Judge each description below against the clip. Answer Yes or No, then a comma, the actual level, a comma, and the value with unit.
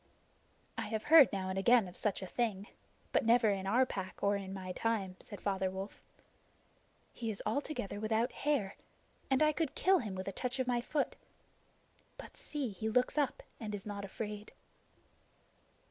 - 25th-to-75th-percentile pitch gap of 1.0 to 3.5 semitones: No, average, 4.3 semitones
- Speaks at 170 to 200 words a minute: Yes, average, 175 wpm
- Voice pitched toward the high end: Yes, high, 215 Hz